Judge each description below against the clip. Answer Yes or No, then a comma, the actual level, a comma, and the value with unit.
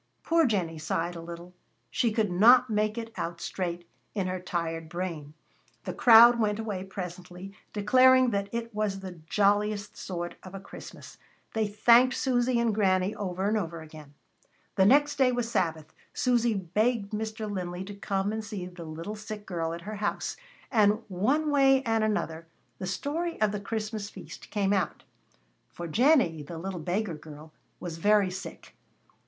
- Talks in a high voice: Yes, high, 200 Hz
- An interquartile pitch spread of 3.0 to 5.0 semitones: Yes, average, 4.1 semitones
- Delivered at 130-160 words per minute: No, average, 170 wpm